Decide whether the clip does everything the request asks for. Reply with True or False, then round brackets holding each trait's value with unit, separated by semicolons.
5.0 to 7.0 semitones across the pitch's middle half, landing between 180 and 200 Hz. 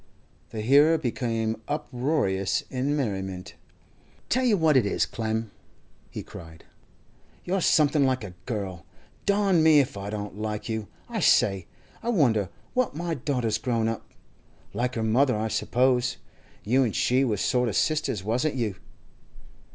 False (5.3 semitones; 120 Hz)